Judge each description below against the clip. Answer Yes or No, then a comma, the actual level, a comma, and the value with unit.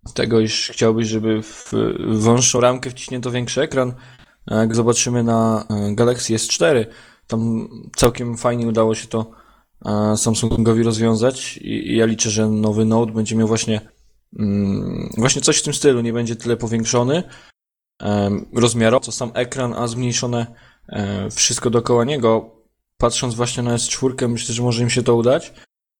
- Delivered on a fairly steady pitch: Yes, narrow, 1.7 semitones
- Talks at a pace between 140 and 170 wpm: Yes, average, 150 wpm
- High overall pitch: No, low, 115 Hz